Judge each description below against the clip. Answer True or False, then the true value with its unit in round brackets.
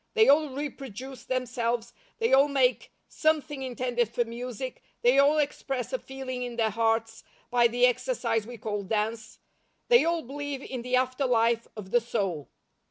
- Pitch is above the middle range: True (250 Hz)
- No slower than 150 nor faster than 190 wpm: True (165 wpm)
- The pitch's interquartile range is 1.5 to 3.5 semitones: True (2.8 semitones)